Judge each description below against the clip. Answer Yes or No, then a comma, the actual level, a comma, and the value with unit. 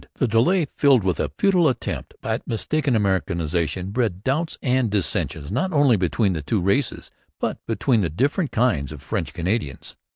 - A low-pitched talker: Yes, low, 115 Hz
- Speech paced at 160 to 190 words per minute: Yes, average, 165 wpm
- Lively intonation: Yes, wide, 7.1 semitones